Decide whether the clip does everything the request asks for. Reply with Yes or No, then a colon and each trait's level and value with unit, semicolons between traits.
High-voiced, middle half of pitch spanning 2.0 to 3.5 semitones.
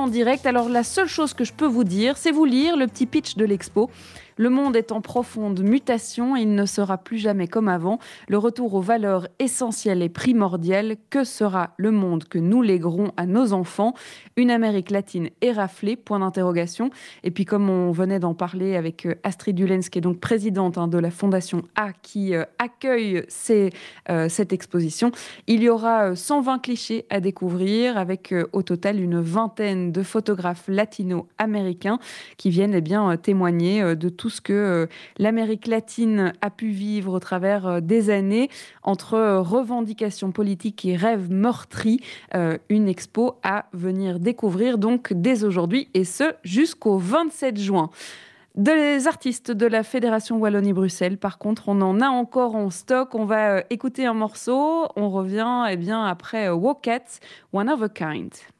No: high, 210 Hz; average, 4.0 semitones